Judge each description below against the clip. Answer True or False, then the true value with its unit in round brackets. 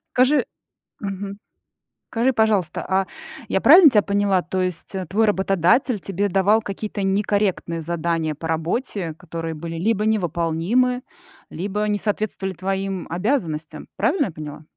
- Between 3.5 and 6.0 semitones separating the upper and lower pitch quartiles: True (3.9 semitones)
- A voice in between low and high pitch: False (195 Hz)